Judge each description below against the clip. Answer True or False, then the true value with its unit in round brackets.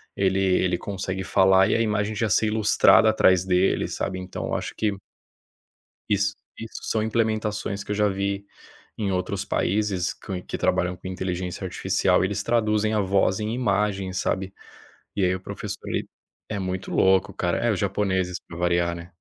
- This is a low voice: True (95 Hz)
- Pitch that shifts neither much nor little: False (2.2 semitones)